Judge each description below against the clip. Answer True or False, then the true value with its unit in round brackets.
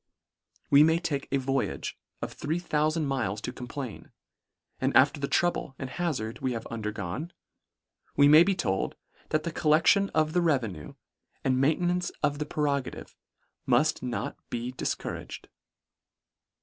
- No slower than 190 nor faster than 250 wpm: False (150 wpm)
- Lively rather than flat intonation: False (4.0 semitones)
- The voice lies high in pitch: False (145 Hz)